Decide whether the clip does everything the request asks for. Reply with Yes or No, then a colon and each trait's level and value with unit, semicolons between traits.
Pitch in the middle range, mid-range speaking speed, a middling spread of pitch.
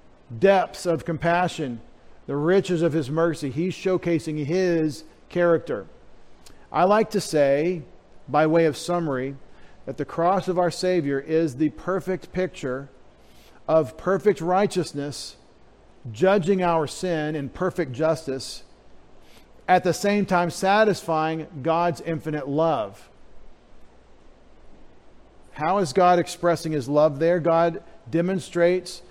No: medium, 165 Hz; slow, 115 wpm; average, 3.1 semitones